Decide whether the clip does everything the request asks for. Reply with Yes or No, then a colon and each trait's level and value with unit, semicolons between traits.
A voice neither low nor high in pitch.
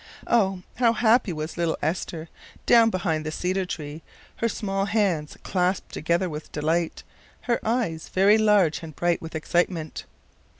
Yes: medium, 180 Hz